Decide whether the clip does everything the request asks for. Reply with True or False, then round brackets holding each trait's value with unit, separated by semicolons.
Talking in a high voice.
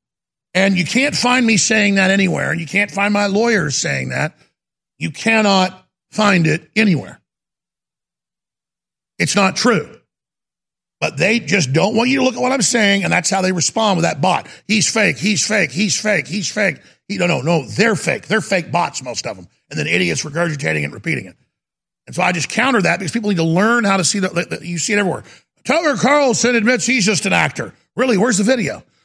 True (200 Hz)